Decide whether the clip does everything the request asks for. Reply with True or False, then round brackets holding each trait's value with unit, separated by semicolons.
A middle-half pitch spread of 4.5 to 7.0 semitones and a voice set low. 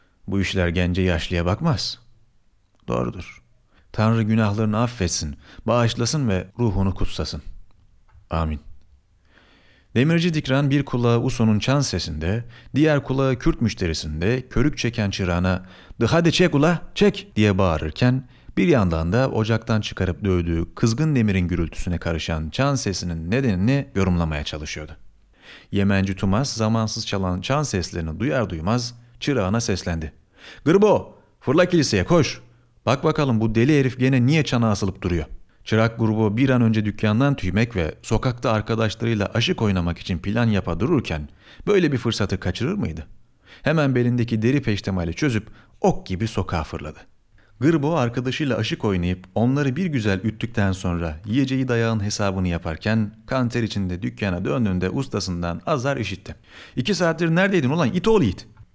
True (5.4 semitones; 110 Hz)